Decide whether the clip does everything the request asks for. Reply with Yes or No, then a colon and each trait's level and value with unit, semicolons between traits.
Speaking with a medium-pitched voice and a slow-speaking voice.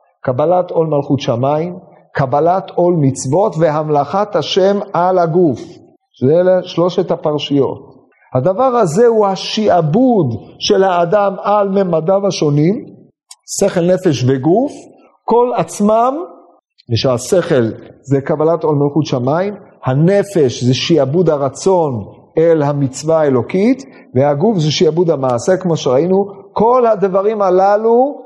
No: medium, 175 Hz; average, 110 wpm